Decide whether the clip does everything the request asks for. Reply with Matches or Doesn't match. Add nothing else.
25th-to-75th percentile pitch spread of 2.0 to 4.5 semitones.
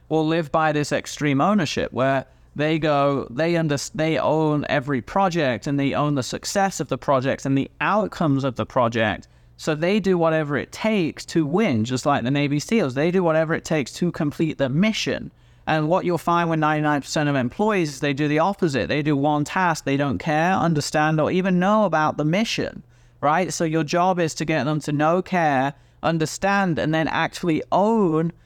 Matches